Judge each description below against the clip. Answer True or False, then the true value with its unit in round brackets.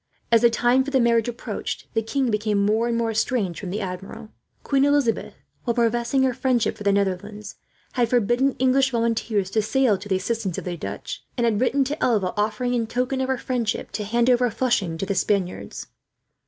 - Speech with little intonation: False (3.3 semitones)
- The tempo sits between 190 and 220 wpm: True (205 wpm)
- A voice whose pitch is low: False (230 Hz)